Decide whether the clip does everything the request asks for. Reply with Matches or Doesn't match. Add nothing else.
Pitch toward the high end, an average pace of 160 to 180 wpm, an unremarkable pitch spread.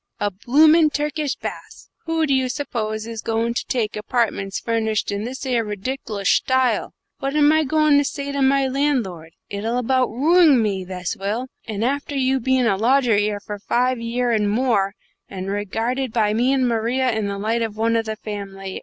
Doesn't match